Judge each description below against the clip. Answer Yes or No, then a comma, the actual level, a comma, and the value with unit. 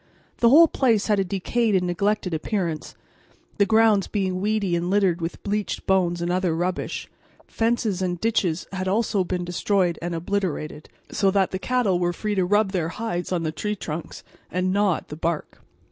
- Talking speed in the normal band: Yes, average, 185 wpm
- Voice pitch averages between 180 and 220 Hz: Yes, high, 190 Hz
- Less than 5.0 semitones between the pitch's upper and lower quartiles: Yes, average, 3.0 semitones